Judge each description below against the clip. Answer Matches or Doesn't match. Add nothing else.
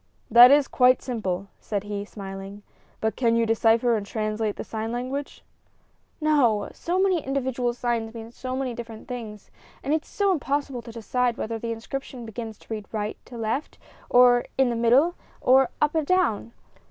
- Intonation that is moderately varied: Matches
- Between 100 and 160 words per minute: Doesn't match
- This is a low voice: Doesn't match